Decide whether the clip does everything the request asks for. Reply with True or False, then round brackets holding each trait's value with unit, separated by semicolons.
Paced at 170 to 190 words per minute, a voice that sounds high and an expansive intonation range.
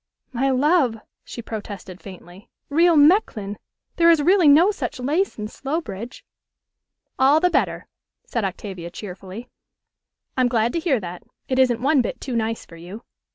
False (155 wpm; 245 Hz; 6.4 semitones)